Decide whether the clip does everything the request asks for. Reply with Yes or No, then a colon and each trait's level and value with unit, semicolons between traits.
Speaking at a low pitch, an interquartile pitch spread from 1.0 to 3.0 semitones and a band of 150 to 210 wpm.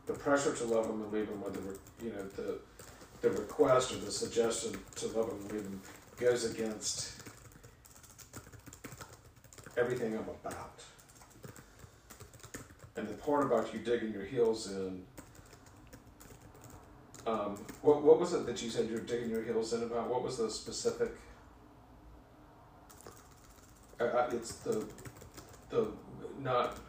No: low, 115 Hz; narrow, 2.5 semitones; slow, 135 wpm